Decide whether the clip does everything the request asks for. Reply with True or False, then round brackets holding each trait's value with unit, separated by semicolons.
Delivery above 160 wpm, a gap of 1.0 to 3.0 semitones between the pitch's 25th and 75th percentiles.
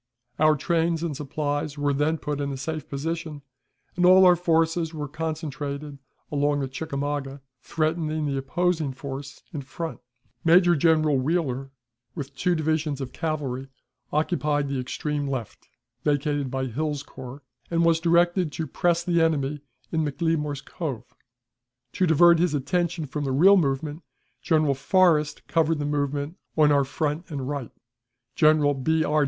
False (150 wpm; 2.5 semitones)